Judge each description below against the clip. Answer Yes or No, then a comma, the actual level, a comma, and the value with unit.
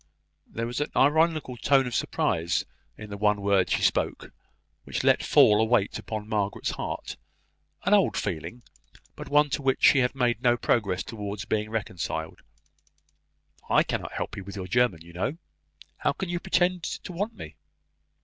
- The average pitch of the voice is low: Yes, low, 115 Hz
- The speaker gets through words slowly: No, average, 170 wpm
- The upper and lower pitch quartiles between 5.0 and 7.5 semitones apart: Yes, wide, 5.6 semitones